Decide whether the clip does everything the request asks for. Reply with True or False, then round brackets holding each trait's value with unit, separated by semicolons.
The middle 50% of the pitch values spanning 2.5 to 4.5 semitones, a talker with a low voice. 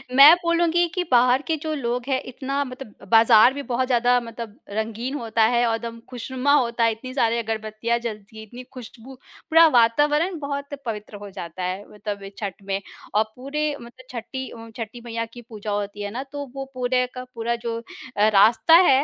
False (3.3 semitones; 235 Hz)